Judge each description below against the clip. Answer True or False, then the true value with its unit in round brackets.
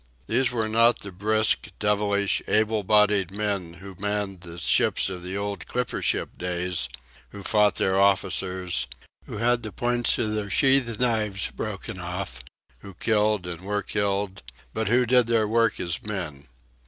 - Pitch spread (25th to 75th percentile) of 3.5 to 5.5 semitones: False (2.6 semitones)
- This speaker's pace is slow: False (160 wpm)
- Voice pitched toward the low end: True (105 Hz)